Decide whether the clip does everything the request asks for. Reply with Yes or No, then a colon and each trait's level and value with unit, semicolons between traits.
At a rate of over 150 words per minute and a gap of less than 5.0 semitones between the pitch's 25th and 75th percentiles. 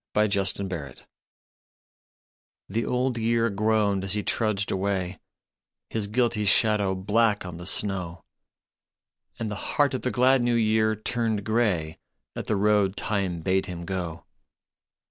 No: slow, 135 wpm; average, 2.9 semitones